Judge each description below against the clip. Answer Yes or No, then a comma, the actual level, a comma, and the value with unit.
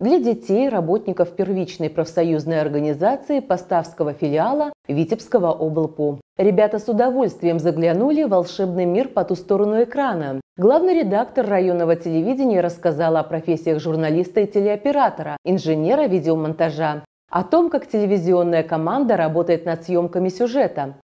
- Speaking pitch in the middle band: Yes, medium, 175 Hz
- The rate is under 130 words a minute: Yes, average, 120 wpm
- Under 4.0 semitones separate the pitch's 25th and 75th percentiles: No, average, 5.0 semitones